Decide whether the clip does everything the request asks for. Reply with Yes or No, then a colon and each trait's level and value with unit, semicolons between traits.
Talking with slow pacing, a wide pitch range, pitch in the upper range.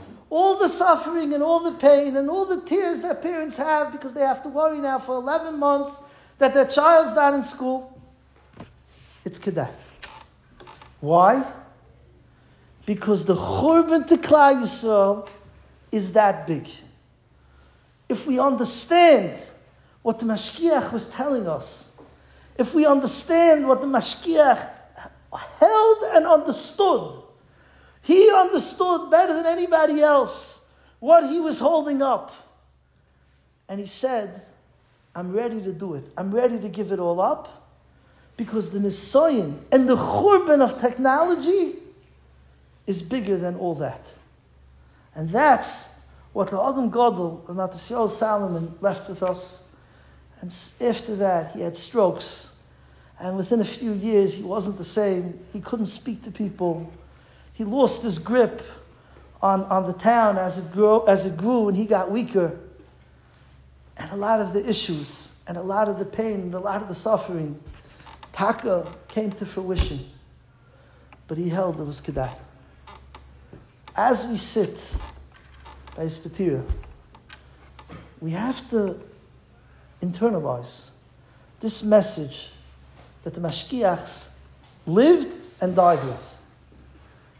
Yes: slow, 130 wpm; wide, 8.6 semitones; high, 210 Hz